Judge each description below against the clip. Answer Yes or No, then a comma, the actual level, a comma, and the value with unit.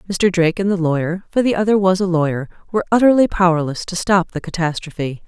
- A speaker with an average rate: Yes, average, 180 wpm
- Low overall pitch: No, medium, 180 Hz